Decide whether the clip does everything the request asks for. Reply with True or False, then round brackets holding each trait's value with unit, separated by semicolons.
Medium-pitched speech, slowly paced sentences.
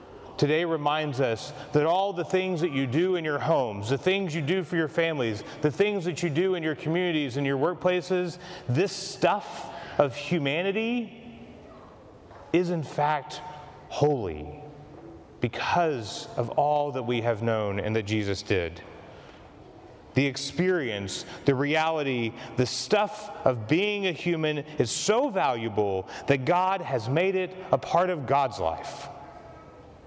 False (150 Hz; 145 wpm)